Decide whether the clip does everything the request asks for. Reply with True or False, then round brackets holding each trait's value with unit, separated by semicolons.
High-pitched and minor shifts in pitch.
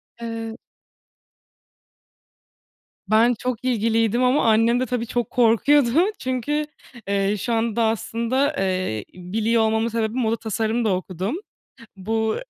True (225 Hz; 1.7 semitones)